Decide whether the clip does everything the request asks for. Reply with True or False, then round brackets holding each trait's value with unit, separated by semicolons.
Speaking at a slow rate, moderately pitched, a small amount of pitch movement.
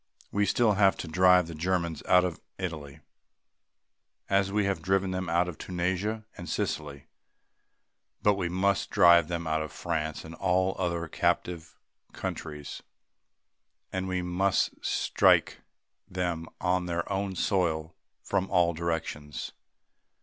False (130 wpm; 90 Hz; 2.2 semitones)